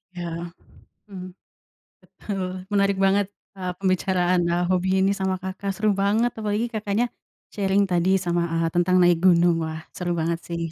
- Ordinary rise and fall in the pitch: No, narrow, 2.2 semitones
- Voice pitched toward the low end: No, medium, 185 Hz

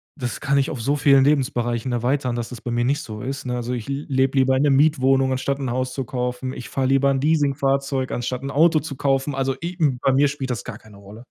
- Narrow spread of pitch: Yes, narrow, 1.9 semitones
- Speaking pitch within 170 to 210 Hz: No, low, 135 Hz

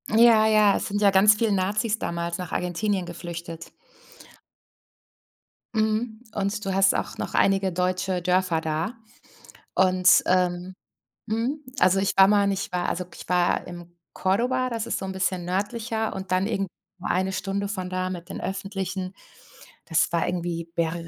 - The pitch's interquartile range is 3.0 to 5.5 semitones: No, narrow, 2.6 semitones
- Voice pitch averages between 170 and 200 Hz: Yes, high, 190 Hz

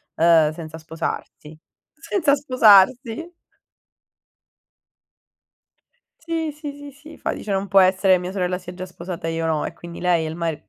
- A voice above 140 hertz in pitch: Yes, medium, 185 Hz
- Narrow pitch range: No, wide, 8.5 semitones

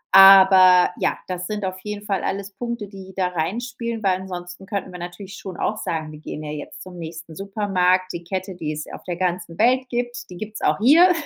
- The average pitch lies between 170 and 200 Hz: Yes, high, 190 Hz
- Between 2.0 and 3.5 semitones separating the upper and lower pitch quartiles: Yes, average, 2.8 semitones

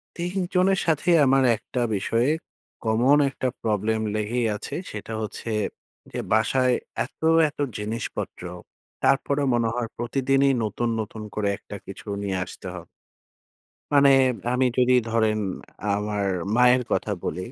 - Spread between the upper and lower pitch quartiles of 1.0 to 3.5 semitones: No, average, 4.0 semitones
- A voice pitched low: Yes, low, 120 Hz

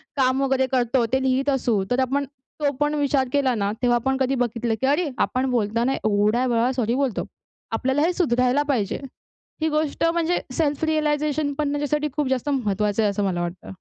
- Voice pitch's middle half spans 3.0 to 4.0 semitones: Yes, average, 3.5 semitones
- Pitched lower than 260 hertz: No, very high, 265 Hz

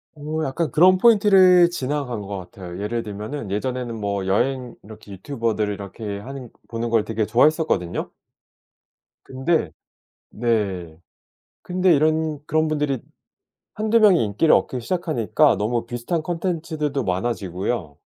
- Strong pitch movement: Yes, wide, 7.2 semitones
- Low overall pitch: Yes, low, 125 Hz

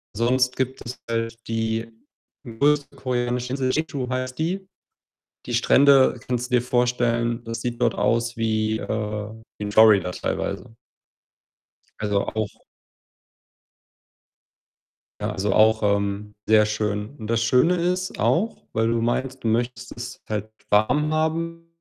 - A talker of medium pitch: No, low, 120 Hz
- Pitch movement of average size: Yes, average, 3.0 semitones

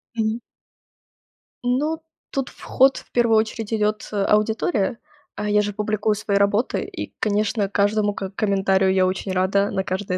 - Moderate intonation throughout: No, narrow, 1.8 semitones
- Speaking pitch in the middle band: No, high, 210 Hz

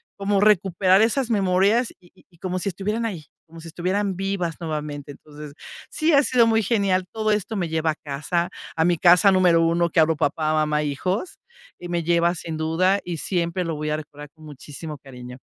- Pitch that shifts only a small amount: No, average, 4.0 semitones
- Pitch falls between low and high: Yes, medium, 175 Hz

